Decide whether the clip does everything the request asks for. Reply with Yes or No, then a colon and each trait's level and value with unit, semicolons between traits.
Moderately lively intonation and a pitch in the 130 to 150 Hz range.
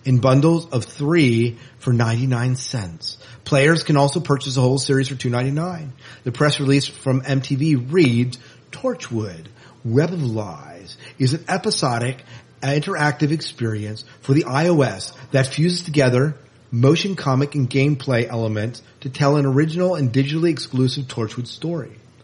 Yes: average, 3.3 semitones; low, 135 Hz